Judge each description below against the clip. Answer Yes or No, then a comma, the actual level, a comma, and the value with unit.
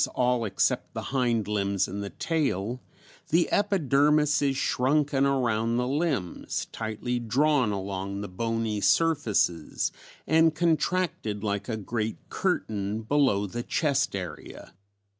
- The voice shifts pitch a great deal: Yes, wide, 6.1 semitones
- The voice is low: Yes, low, 120 Hz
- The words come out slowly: Yes, slow, 125 wpm